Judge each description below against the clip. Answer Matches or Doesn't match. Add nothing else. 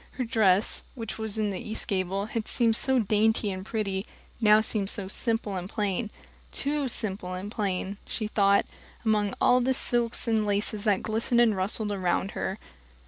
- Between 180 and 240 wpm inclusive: Doesn't match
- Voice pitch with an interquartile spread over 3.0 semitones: Doesn't match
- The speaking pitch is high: Matches